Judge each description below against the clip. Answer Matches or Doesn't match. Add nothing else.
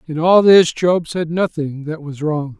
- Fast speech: Matches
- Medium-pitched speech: Matches